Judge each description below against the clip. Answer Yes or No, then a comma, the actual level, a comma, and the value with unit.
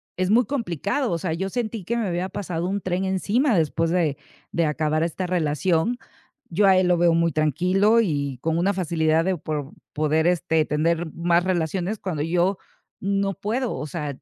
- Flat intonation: No, average, 3.4 semitones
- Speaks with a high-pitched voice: No, medium, 175 Hz